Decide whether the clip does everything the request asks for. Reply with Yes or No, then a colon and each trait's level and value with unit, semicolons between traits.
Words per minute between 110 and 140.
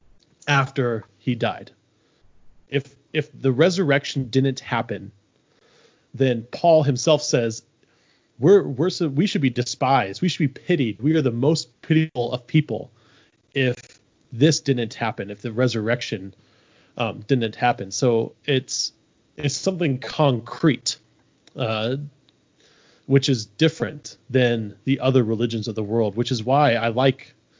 Yes: slow, 135 wpm